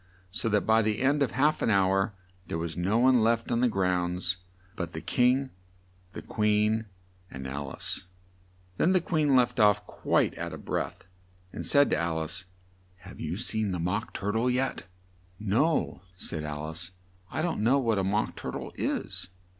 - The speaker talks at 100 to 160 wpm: No, average, 185 wpm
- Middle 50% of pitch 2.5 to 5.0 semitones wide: No, wide, 5.6 semitones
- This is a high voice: No, low, 105 Hz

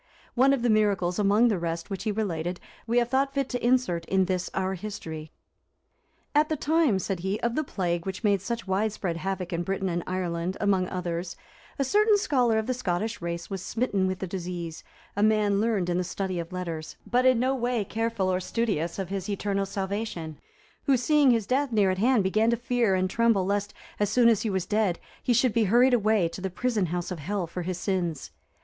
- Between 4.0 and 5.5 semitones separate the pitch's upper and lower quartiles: Yes, average, 4.4 semitones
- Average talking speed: No, fast, 215 wpm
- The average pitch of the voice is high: Yes, high, 200 Hz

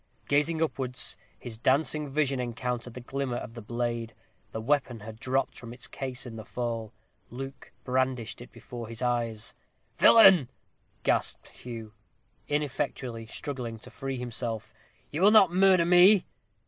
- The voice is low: Yes, low, 125 Hz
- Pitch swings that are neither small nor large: Yes, average, 3.4 semitones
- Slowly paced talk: No, average, 145 wpm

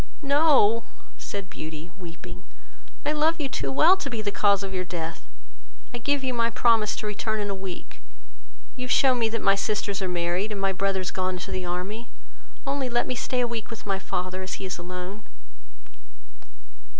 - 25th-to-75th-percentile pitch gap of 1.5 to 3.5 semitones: No, average, 4.5 semitones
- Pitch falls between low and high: No, high, 205 Hz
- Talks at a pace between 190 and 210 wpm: Yes, average, 195 wpm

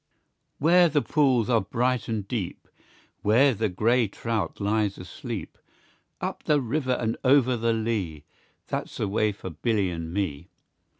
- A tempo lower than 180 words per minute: Yes, average, 145 wpm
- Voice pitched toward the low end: Yes, low, 115 Hz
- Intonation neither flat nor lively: Yes, average, 4.2 semitones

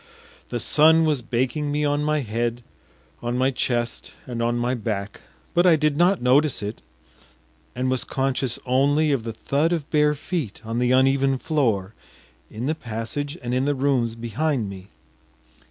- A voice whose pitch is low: Yes, low, 130 Hz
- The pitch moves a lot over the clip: No, average, 4.0 semitones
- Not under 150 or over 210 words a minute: Yes, average, 170 wpm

